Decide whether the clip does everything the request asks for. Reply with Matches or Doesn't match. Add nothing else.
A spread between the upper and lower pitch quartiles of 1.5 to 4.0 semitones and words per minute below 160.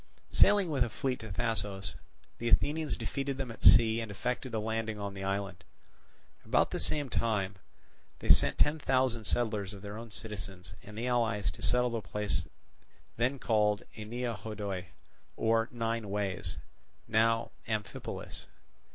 Matches